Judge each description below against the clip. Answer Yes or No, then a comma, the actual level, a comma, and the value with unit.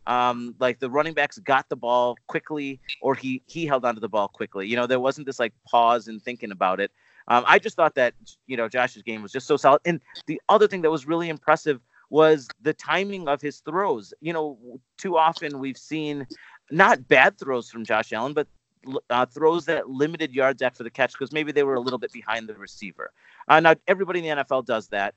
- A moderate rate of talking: No, fast, 225 wpm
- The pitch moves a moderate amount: Yes, average, 4.3 semitones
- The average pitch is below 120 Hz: No, low, 135 Hz